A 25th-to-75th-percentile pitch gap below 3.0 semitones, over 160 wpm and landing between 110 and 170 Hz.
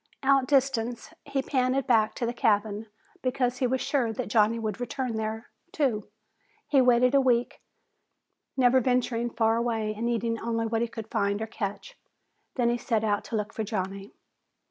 No: narrow, 2.4 semitones; average, 170 wpm; high, 235 Hz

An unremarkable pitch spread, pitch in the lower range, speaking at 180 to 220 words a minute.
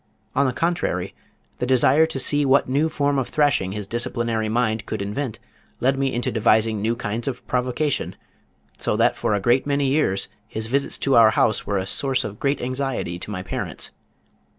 Yes: average, 4.1 semitones; low, 125 Hz; average, 190 wpm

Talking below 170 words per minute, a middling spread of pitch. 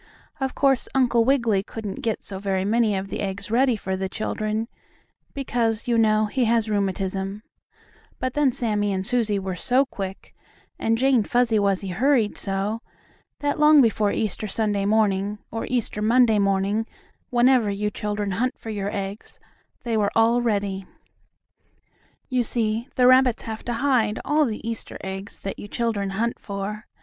Yes: average, 160 wpm; average, 3.2 semitones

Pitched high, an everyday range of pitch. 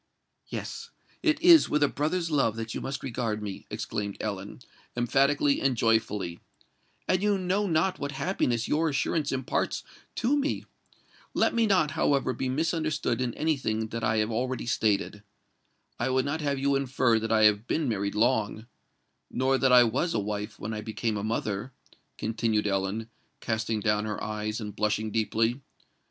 No: low, 120 Hz; average, 4.7 semitones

